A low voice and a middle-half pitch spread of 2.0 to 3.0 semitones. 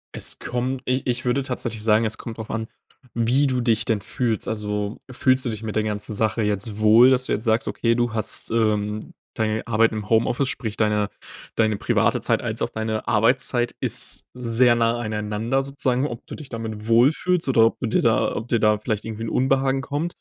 Yes: low, 115 Hz; narrow, 2.6 semitones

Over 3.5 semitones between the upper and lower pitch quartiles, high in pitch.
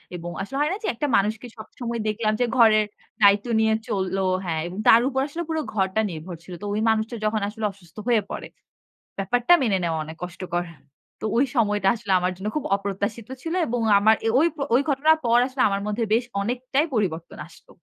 Yes: average, 4.1 semitones; high, 215 Hz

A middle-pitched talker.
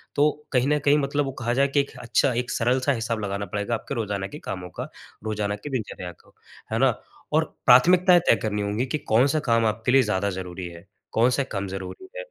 No: low, 115 Hz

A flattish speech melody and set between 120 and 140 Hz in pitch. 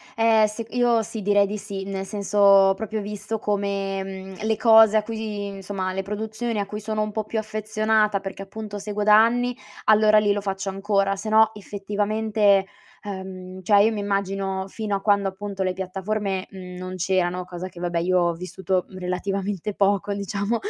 No: narrow, 1.9 semitones; high, 200 Hz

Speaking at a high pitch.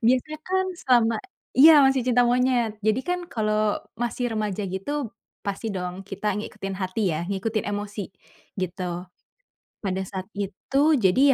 Yes: high, 215 Hz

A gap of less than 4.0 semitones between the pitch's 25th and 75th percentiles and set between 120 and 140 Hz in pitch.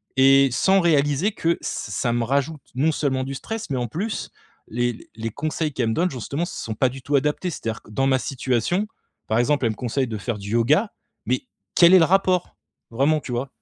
No: average, 4.9 semitones; low, 135 Hz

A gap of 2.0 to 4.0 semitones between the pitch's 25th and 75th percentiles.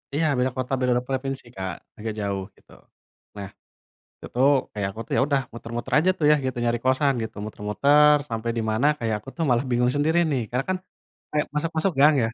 No: average, 4.5 semitones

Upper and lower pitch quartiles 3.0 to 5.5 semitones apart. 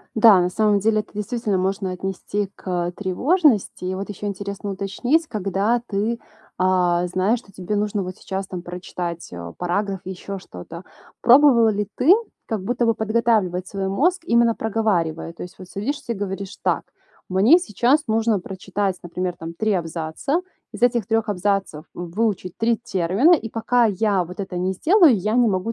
Yes: average, 3.6 semitones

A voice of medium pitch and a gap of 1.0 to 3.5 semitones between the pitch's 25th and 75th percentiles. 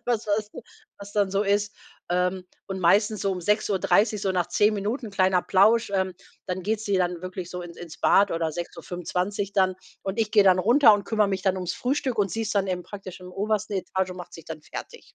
No: high, 195 Hz; narrow, 2.5 semitones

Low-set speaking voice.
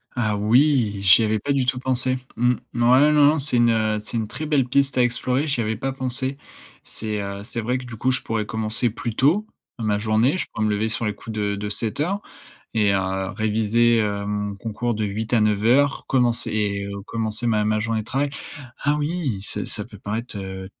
Yes: low, 115 Hz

